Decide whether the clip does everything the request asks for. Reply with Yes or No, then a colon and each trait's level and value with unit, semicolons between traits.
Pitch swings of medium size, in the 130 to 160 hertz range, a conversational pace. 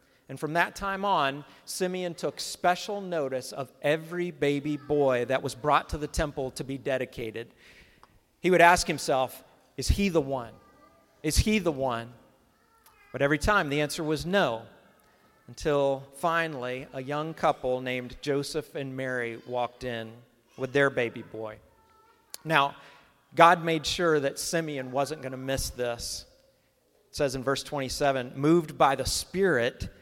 Yes: average, 4.1 semitones; medium, 140 Hz; average, 150 wpm